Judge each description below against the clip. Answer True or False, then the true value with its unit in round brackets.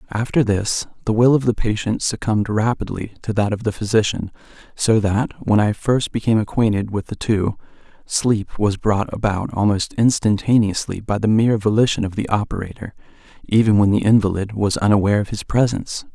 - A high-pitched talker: False (105 Hz)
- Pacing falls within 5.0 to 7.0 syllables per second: True (5.5 syllables/s)